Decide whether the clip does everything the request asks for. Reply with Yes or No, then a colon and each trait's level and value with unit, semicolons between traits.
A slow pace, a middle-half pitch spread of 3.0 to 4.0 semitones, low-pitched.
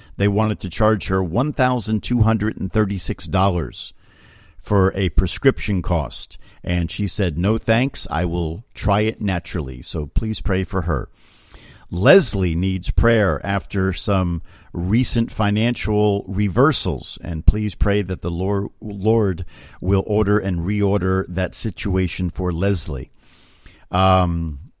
Yes: slow, 115 wpm; average, 3.3 semitones; very low, 95 Hz